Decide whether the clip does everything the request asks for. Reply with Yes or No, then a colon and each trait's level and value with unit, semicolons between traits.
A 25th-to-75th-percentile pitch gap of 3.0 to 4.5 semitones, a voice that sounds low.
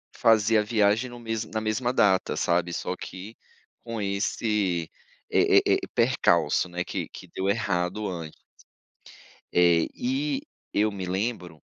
Yes: average, 4.1 semitones; low, 105 Hz